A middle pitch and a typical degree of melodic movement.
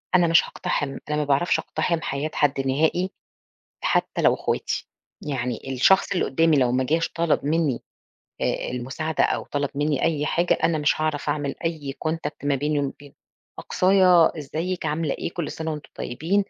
Yes: medium, 150 Hz; average, 3.0 semitones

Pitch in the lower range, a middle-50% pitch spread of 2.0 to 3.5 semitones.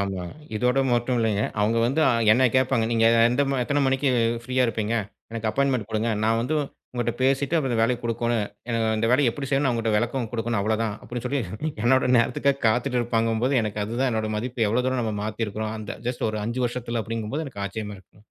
Yes: low, 115 Hz; average, 2.7 semitones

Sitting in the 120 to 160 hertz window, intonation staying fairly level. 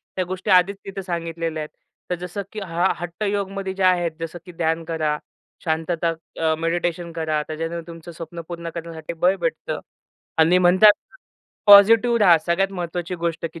No: medium, 170 Hz; narrow, 2.1 semitones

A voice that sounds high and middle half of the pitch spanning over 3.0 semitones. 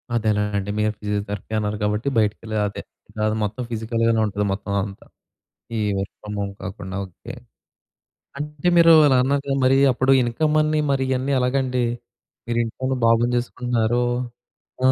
No: low, 115 Hz; average, 3.9 semitones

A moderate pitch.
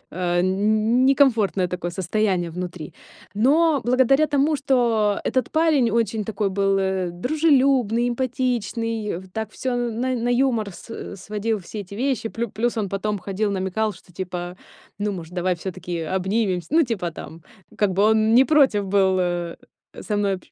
No: high, 215 Hz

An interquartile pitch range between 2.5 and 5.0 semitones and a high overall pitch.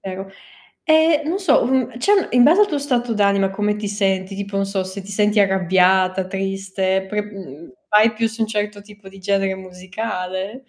Yes: average, 2.8 semitones; high, 200 Hz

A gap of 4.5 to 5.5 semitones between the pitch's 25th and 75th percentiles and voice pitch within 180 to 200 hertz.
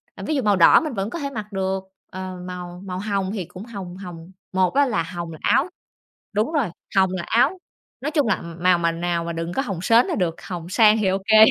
No: average, 3.9 semitones; high, 190 Hz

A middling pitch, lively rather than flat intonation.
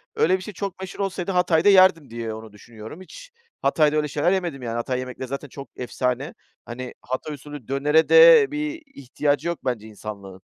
Yes: medium, 145 Hz; wide, 6.9 semitones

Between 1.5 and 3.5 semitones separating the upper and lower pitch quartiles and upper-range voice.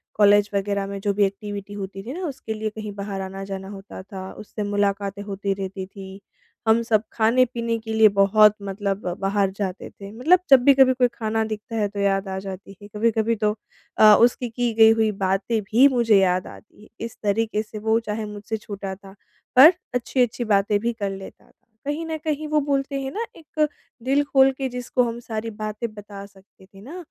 Yes: average, 3.0 semitones; high, 215 Hz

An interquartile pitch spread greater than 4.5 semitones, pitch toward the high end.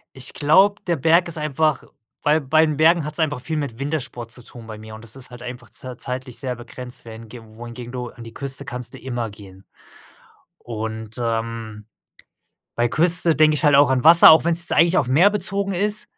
No: average, 5.2 semitones; low, 130 Hz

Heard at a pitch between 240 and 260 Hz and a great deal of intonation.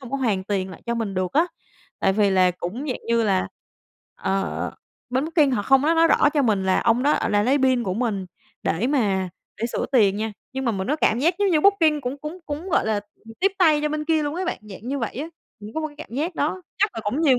Yes: very high, 255 Hz; wide, 6.6 semitones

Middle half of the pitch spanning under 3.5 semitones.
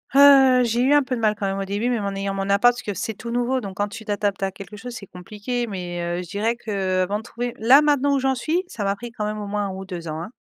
No: average, 3.8 semitones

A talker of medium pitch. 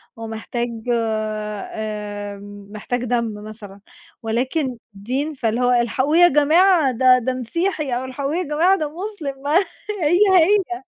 No: very high, 255 Hz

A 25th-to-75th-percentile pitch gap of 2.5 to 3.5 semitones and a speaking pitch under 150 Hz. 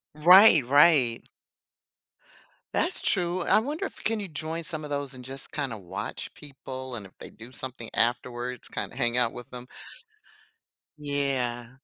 No: average, 4.2 semitones; low, 135 Hz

